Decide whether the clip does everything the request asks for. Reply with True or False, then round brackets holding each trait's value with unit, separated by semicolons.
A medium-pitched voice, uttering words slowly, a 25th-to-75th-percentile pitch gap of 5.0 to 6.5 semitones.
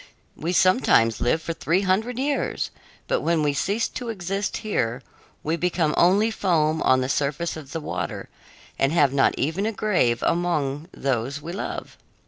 False (165 Hz; 165 wpm; 5.5 semitones)